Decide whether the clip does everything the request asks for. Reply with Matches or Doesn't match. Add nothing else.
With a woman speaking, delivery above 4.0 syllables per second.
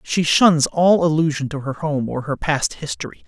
Doesn't match